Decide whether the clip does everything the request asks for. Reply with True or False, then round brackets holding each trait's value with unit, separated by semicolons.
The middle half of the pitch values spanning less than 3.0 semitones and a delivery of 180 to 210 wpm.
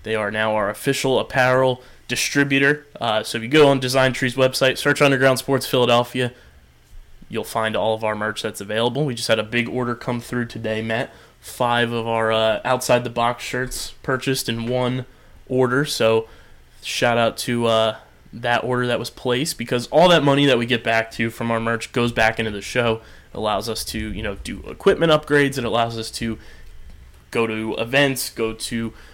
True (2.6 semitones; 200 wpm)